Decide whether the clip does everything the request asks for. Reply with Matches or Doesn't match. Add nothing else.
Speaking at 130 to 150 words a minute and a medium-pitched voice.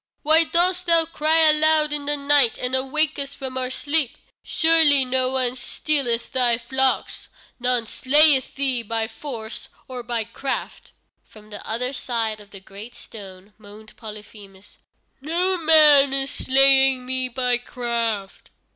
Doesn't match